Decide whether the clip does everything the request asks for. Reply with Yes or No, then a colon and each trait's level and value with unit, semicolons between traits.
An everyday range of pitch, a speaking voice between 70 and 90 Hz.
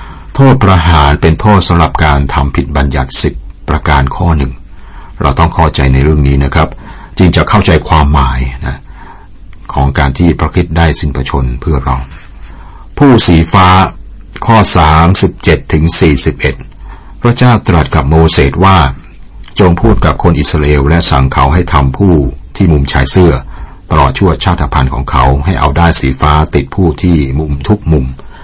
Yes: average, 4.5 semitones; very low, 80 Hz